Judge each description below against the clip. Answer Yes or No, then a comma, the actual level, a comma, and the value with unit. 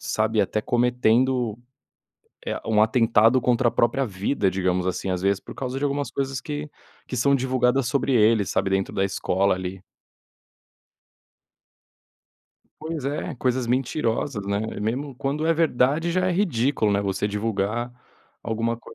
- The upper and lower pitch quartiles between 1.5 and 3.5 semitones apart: No, average, 4.7 semitones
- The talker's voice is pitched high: No, low, 120 Hz